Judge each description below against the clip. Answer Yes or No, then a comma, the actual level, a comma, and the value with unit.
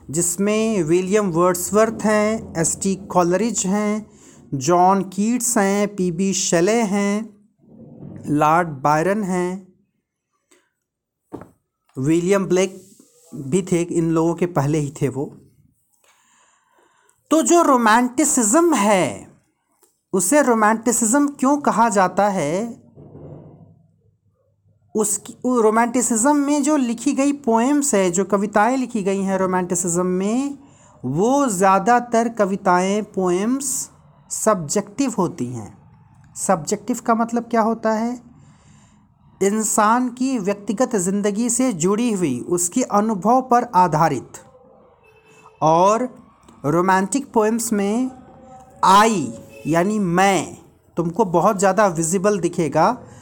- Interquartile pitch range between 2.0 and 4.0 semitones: No, average, 4.7 semitones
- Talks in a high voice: Yes, high, 205 Hz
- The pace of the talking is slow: Yes, slow, 100 wpm